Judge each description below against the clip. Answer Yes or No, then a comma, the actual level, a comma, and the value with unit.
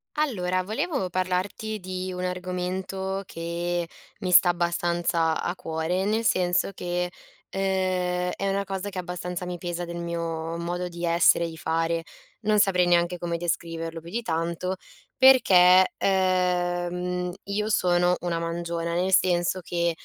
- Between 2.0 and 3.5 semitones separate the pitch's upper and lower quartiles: No, narrow, 1.4 semitones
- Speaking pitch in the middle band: Yes, medium, 180 Hz